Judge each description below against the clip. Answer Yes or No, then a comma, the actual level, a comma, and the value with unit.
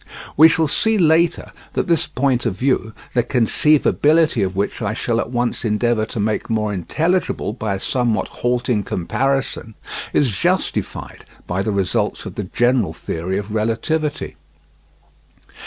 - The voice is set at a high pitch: No, low, 120 Hz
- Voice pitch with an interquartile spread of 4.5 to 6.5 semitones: Yes, average, 4.9 semitones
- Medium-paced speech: Yes, average, 145 wpm